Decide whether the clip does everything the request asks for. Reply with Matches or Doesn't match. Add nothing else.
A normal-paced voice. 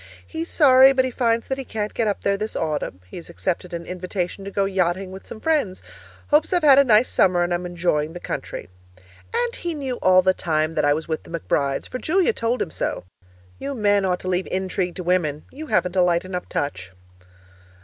Doesn't match